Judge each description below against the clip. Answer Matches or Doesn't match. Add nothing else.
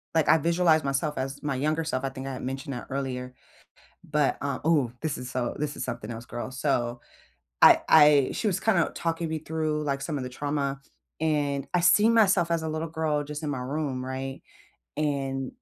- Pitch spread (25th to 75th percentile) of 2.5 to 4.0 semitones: Matches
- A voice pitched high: Doesn't match